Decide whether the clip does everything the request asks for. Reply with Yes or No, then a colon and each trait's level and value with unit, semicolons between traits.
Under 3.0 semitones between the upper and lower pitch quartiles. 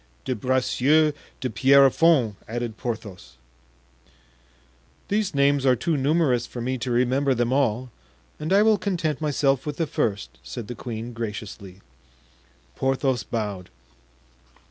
No: average, 3.6 semitones